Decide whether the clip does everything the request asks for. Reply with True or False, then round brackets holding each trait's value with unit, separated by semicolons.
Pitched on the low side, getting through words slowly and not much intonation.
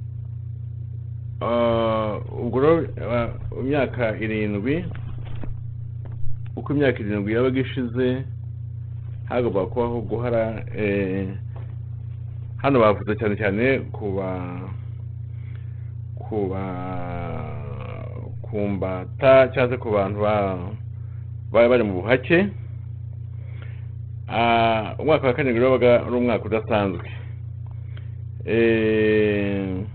True (115 Hz; 80 wpm; 1.1 semitones)